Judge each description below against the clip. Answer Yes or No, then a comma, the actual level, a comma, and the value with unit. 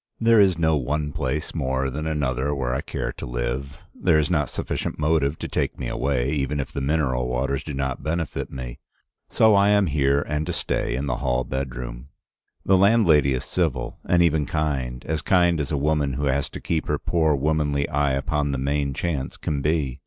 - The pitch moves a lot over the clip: No, average, 2.8 semitones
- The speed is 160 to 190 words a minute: No, fast, 205 wpm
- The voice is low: Yes, very low, 70 Hz